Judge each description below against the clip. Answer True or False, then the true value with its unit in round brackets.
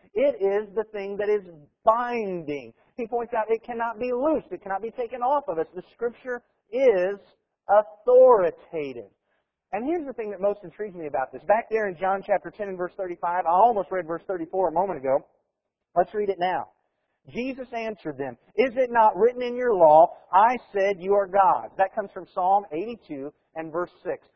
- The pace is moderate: True (195 wpm)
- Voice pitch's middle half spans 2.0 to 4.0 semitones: False (4.7 semitones)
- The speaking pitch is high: True (205 Hz)